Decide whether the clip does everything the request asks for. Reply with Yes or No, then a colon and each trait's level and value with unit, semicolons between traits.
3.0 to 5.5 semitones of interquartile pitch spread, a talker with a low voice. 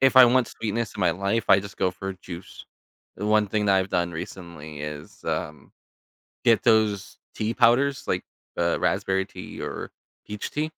Yes: average, 4.2 semitones; low, 100 Hz